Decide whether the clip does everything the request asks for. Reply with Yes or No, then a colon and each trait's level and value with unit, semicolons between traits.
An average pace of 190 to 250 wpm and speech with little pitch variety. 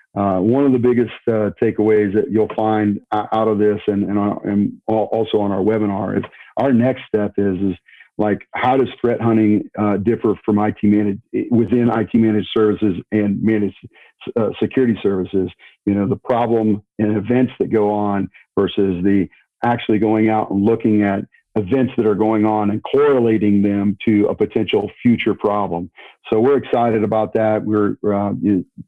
No: average, 175 wpm; narrow, 1.6 semitones